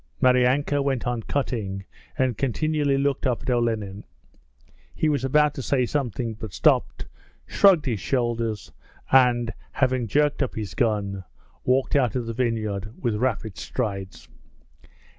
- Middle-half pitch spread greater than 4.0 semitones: No, average, 3.6 semitones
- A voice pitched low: Yes, low, 125 Hz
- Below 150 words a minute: Yes, average, 140 wpm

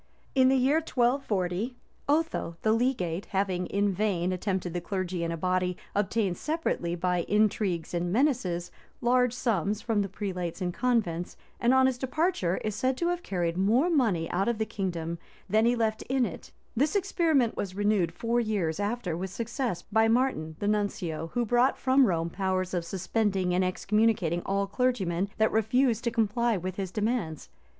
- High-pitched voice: Yes, high, 205 Hz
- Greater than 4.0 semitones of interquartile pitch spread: Yes, average, 5.1 semitones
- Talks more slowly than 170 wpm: No, average, 175 wpm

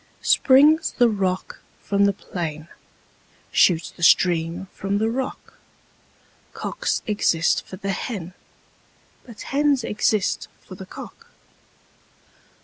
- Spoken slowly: Yes, slow, 110 wpm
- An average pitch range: Yes, average, 4.7 semitones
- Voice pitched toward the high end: Yes, high, 200 Hz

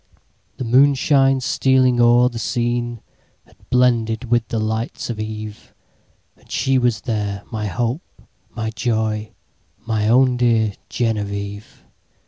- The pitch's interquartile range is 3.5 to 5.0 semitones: No, narrow, 2.4 semitones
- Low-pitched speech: Yes, low, 115 Hz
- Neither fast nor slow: No, slow, 110 wpm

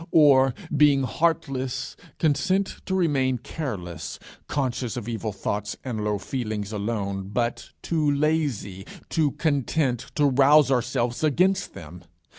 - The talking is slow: Yes, slow, 120 wpm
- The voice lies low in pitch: Yes, low, 130 Hz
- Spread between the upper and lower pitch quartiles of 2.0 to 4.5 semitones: No, wide, 5.4 semitones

